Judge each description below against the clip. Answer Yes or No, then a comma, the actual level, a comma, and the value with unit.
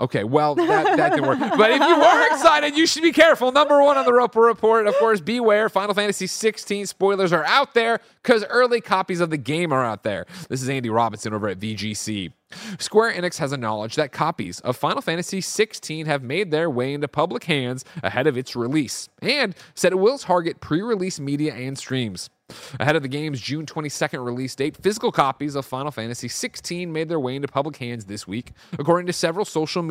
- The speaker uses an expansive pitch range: Yes, wide, 8.2 semitones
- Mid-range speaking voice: Yes, medium, 160 Hz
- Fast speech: Yes, fast, 215 wpm